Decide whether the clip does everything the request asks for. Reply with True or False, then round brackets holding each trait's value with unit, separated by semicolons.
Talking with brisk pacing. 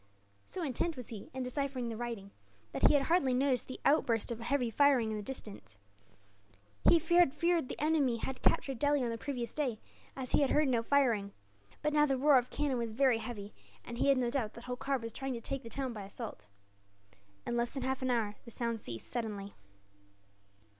True (210 wpm)